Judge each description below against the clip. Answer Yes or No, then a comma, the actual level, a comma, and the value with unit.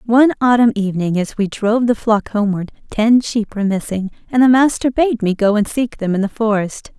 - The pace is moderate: No, fast, 215 wpm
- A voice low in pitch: No, high, 220 Hz